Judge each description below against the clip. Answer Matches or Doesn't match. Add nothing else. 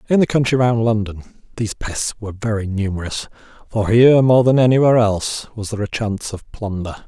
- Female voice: Doesn't match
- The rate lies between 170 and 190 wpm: Matches